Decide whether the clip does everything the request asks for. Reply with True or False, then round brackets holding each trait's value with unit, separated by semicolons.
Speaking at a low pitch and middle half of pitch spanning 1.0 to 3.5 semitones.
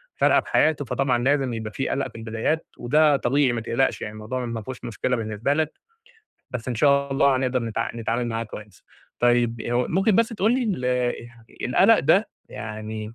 False (125 Hz; 3.9 semitones)